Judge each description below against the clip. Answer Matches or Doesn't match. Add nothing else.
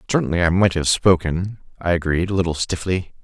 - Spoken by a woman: Doesn't match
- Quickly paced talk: Doesn't match